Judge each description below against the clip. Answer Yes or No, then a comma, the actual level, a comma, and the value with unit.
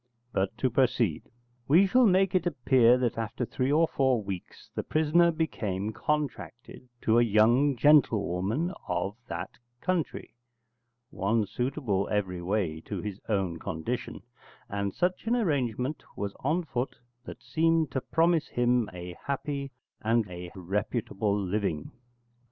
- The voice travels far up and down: Yes, wide, 6.9 semitones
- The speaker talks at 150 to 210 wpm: No, slow, 135 wpm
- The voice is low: Yes, low, 120 Hz